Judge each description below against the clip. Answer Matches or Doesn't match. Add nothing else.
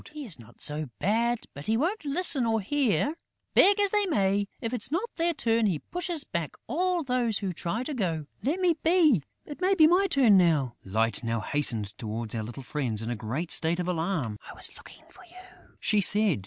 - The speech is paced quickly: Matches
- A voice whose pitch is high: Matches